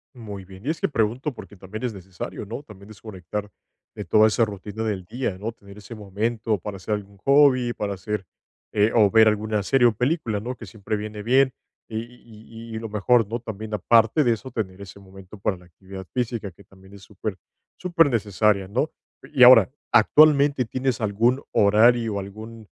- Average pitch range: Yes, average, 3.1 semitones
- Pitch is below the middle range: Yes, low, 110 Hz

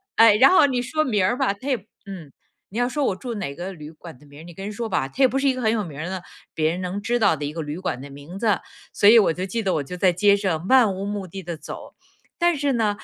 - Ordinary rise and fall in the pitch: No, wide, 5.7 semitones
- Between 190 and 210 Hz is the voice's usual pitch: Yes, high, 195 Hz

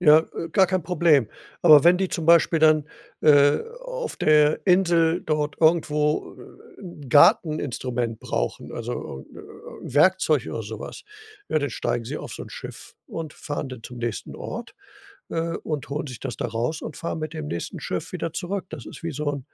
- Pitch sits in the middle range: Yes, medium, 155 Hz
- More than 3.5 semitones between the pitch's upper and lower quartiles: No, average, 3.1 semitones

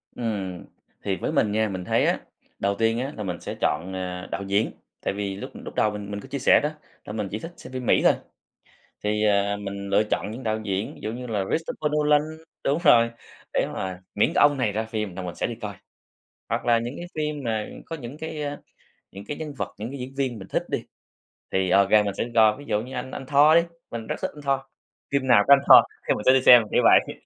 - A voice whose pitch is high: No, low, 110 Hz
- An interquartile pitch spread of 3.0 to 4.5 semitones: No, average, 5.1 semitones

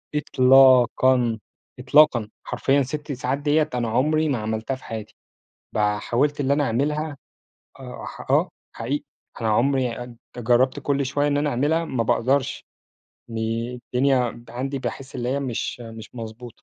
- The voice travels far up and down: No, average, 3.3 semitones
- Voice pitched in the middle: No, low, 130 Hz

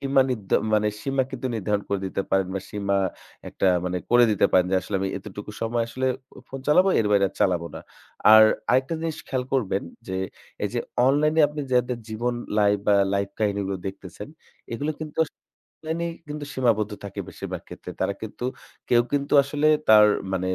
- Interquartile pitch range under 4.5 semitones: No, average, 5.2 semitones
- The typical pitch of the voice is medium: No, low, 110 Hz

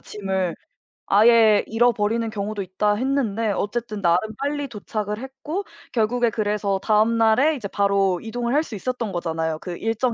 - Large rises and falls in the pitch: No, average, 3.2 semitones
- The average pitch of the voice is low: No, high, 215 Hz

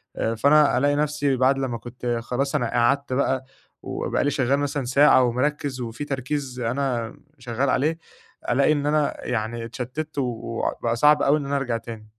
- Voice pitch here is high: No, low, 130 Hz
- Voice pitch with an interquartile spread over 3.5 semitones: No, average, 3.1 semitones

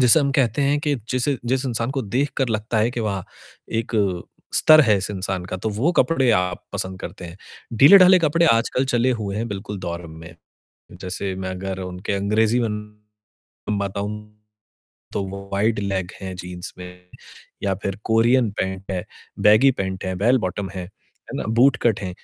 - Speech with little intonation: No, average, 4.3 semitones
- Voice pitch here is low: Yes, low, 105 Hz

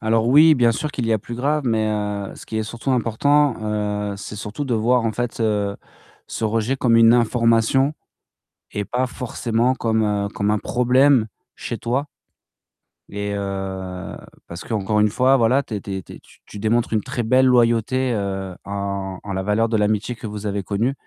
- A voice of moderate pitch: No, low, 115 Hz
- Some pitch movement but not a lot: Yes, average, 3.2 semitones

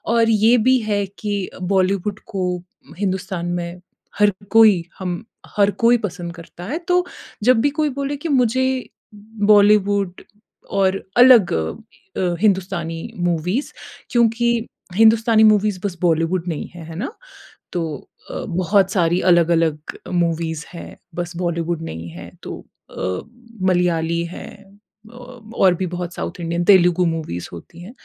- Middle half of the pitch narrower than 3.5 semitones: No, average, 3.8 semitones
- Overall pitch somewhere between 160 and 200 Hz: Yes, medium, 185 Hz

